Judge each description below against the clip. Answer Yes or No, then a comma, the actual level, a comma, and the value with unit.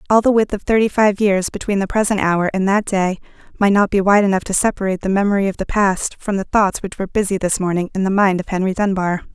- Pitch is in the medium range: No, high, 195 Hz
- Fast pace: Yes, fast, 255 wpm